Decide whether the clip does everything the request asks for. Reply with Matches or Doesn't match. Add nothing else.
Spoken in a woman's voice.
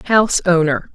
Matches